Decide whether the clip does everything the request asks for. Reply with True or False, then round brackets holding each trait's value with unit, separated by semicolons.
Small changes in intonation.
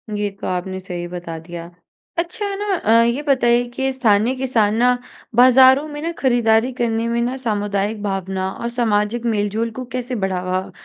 False (4.2 semitones)